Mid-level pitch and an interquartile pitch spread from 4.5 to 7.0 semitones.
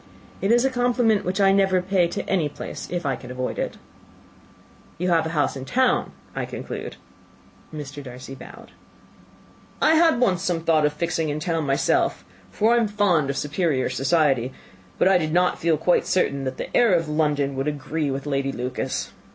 Yes: medium, 160 Hz; wide, 5.4 semitones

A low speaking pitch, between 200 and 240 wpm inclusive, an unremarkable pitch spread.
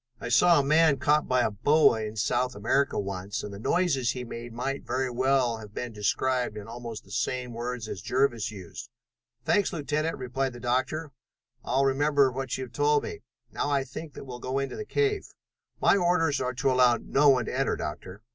Yes: low, 130 Hz; fast, 205 wpm; average, 3.3 semitones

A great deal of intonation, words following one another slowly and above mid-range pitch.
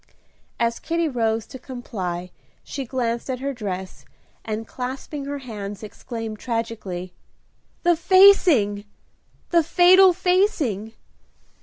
Yes: wide, 6.2 semitones; slow, 110 wpm; high, 240 Hz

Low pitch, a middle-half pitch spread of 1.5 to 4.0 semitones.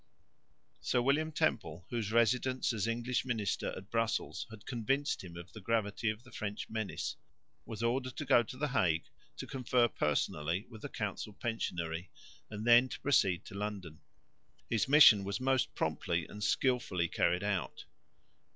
No: low, 110 Hz; average, 4.7 semitones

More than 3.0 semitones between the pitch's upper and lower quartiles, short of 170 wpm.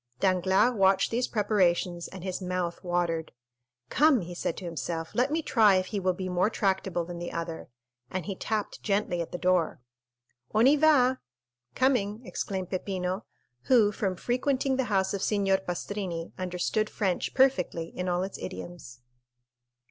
Yes: average, 3.4 semitones; average, 160 wpm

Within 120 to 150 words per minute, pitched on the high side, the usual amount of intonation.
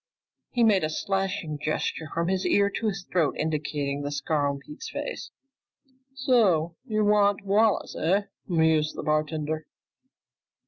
No: average, 140 wpm; medium, 165 Hz; average, 4.7 semitones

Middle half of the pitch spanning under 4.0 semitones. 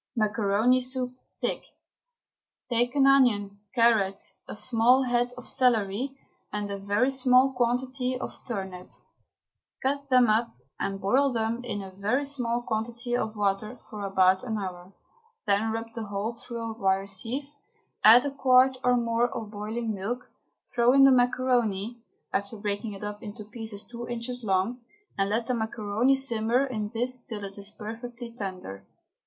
Yes: average, 3.3 semitones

